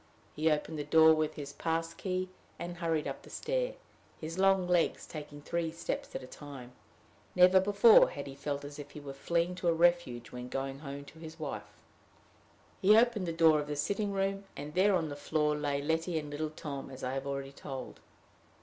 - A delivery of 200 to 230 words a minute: Yes, fast, 205 wpm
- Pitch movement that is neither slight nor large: Yes, average, 3.6 semitones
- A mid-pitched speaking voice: Yes, medium, 155 Hz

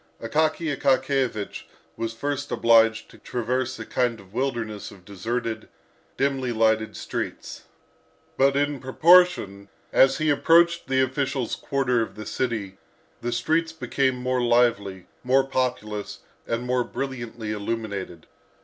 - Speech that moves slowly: Yes, slow, 125 wpm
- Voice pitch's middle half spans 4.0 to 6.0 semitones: No, average, 3.4 semitones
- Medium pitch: No, low, 125 Hz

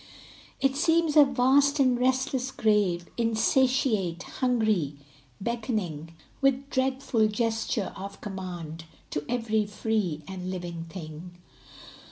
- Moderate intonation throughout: No, wide, 6.3 semitones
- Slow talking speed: Yes, slow, 105 wpm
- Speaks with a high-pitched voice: Yes, high, 220 Hz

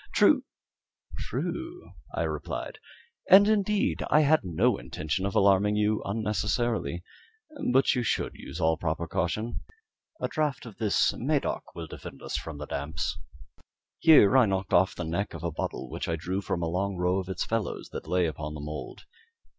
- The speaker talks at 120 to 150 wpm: No, average, 170 wpm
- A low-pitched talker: Yes, very low, 95 Hz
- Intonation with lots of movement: Yes, wide, 6.2 semitones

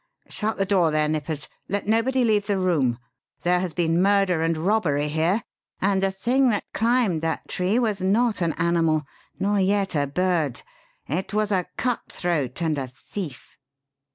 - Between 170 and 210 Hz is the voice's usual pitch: Yes, medium, 185 Hz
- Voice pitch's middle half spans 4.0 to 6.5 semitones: Yes, average, 4.4 semitones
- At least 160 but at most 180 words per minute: Yes, average, 170 wpm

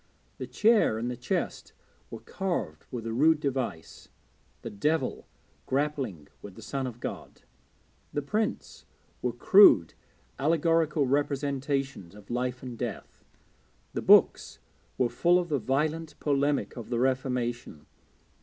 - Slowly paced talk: Yes, slow, 130 wpm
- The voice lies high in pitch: No, low, 135 Hz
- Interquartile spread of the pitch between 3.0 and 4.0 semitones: Yes, average, 3.7 semitones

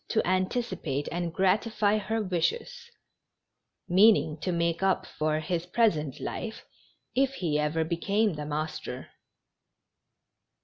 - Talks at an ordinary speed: No, slow, 115 wpm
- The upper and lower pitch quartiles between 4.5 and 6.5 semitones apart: Yes, average, 5.1 semitones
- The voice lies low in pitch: No, medium, 180 Hz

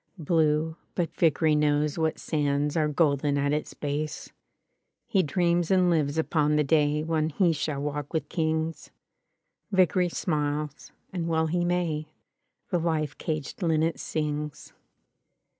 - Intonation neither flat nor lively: No, narrow, 1.8 semitones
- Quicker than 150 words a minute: No, average, 140 wpm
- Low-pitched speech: No, medium, 155 Hz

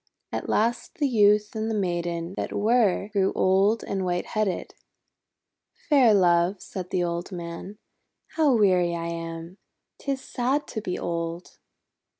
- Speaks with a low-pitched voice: No, high, 190 Hz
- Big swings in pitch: No, average, 4.0 semitones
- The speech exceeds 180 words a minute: No, average, 145 wpm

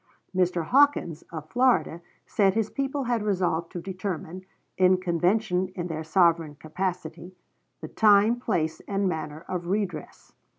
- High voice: No, medium, 180 Hz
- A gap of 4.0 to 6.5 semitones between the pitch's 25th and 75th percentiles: No, average, 3.6 semitones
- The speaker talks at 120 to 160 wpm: Yes, slow, 135 wpm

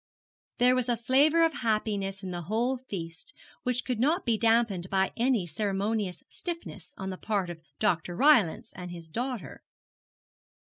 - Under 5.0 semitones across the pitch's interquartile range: No, wide, 5.5 semitones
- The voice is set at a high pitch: Yes, high, 215 Hz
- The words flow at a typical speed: Yes, average, 160 wpm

